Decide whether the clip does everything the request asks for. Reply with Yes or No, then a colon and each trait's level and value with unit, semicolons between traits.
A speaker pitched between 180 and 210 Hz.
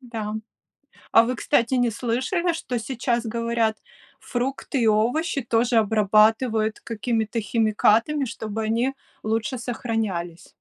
No: high, 230 Hz